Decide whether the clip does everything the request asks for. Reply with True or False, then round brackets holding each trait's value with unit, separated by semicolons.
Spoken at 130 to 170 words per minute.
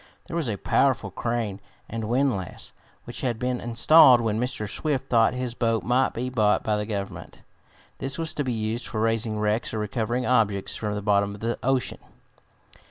False (185 wpm)